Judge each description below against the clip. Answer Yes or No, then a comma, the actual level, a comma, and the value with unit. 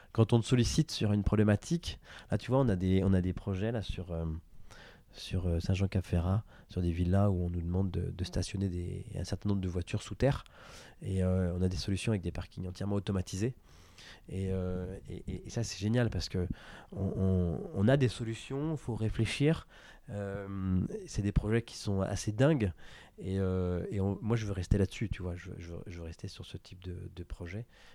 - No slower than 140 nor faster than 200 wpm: No, average, 215 wpm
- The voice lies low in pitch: Yes, very low, 95 Hz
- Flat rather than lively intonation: No, average, 3.0 semitones